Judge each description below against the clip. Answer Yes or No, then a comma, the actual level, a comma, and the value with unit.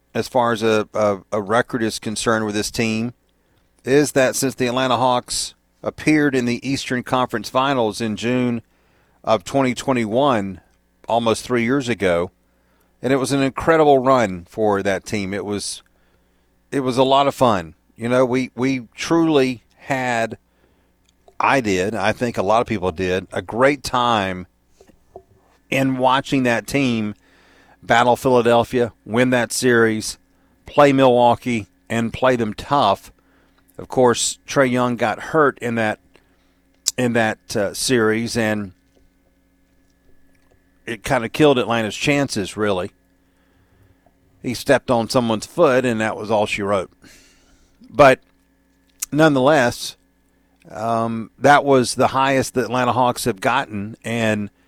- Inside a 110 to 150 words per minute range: Yes, average, 140 wpm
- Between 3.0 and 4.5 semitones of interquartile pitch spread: No, average, 5.2 semitones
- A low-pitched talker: Yes, low, 115 Hz